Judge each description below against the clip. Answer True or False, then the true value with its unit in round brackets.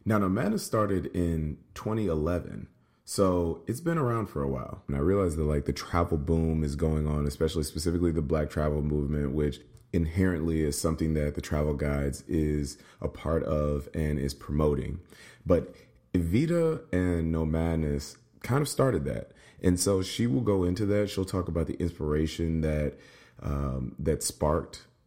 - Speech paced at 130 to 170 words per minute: True (165 wpm)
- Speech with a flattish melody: False (3.6 semitones)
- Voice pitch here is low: True (80 Hz)